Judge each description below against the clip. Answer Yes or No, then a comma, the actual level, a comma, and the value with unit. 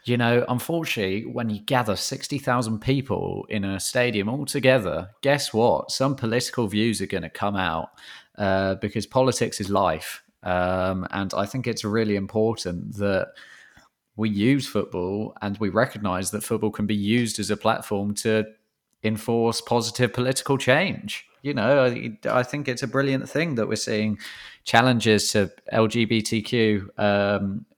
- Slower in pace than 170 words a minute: Yes, average, 155 wpm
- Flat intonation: No, average, 3.3 semitones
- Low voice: Yes, low, 110 Hz